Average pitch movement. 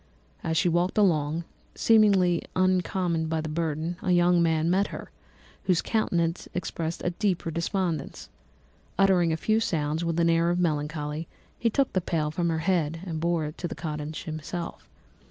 No: narrow, 2.1 semitones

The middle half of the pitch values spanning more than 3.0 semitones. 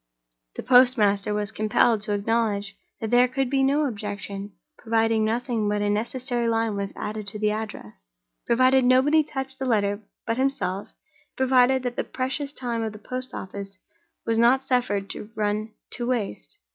Yes: average, 3.6 semitones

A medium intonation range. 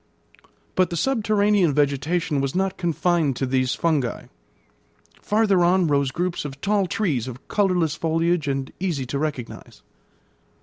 Yes: average, 5.0 semitones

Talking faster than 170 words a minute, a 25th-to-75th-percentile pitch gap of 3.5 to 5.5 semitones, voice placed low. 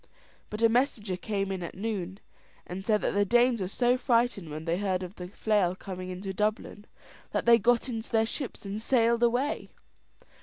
No: average, 190 wpm; average, 3.9 semitones; high, 210 Hz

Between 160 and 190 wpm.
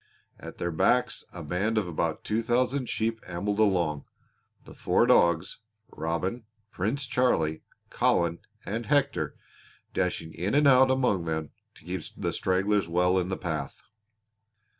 No: average, 140 wpm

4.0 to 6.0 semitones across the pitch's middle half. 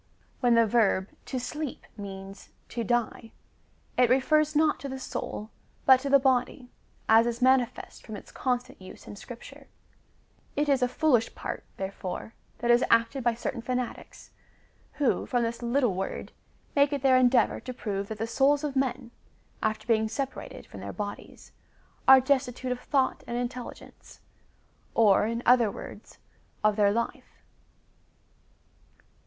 No: average, 2.9 semitones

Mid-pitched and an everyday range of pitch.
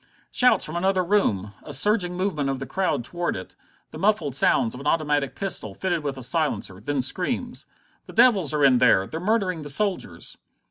No: medium, 155 Hz; wide, 5.9 semitones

